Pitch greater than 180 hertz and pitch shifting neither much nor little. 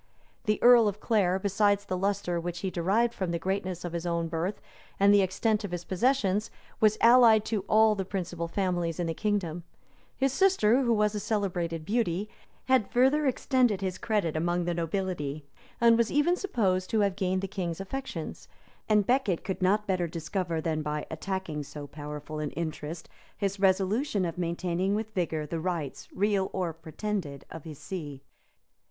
Yes: high, 190 Hz; average, 3.9 semitones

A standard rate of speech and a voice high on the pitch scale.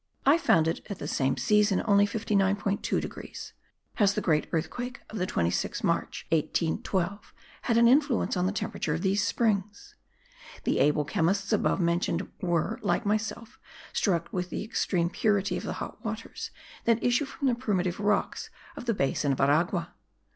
Yes: average, 165 wpm; high, 200 Hz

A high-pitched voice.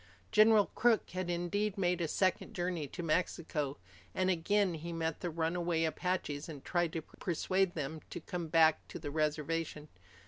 No: medium, 170 Hz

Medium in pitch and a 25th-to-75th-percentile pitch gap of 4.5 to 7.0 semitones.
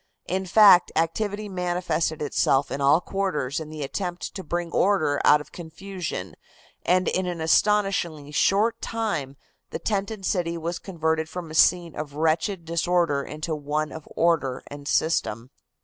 No: medium, 170 Hz; average, 3.7 semitones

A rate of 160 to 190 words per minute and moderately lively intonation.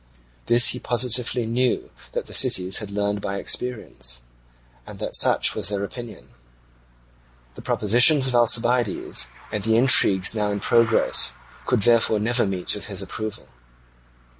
No: average, 140 wpm; average, 3.1 semitones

